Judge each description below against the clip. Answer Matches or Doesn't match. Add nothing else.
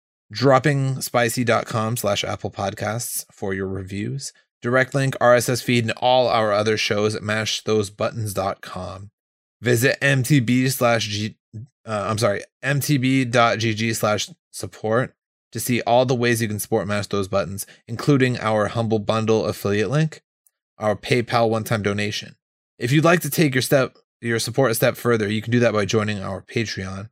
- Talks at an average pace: Matches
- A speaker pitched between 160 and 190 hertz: Doesn't match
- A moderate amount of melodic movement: Matches